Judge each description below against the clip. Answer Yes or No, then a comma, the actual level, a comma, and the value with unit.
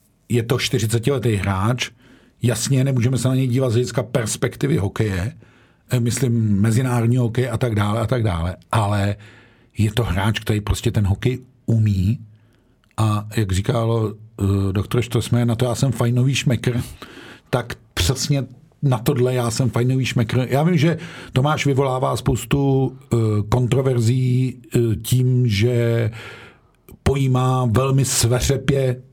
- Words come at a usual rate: Yes, average, 130 wpm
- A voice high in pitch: No, low, 120 Hz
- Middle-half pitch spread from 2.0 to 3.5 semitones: Yes, narrow, 2.6 semitones